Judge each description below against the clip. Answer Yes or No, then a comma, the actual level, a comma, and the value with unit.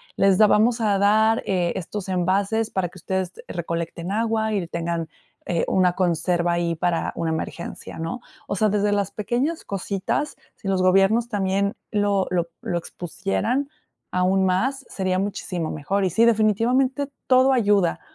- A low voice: No, high, 195 Hz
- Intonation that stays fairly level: No, average, 3.6 semitones